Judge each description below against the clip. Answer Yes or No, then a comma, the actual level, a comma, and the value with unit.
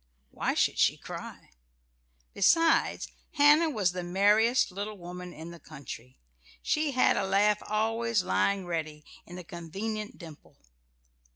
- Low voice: No, high, 195 Hz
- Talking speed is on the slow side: Yes, slow, 130 wpm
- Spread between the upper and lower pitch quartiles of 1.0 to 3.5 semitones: No, average, 4.5 semitones